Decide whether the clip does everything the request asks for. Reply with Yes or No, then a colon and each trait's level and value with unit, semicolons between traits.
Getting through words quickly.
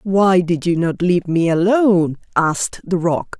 No: average, 175 wpm